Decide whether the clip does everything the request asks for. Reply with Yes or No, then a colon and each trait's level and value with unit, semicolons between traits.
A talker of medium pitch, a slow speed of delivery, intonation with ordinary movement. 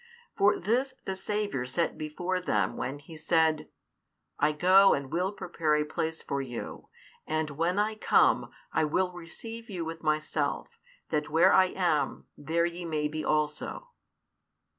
No: medium, 165 Hz; average, 155 wpm; average, 3.7 semitones